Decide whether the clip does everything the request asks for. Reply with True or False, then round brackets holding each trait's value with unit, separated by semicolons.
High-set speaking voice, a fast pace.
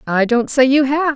True (265 Hz; 260 wpm)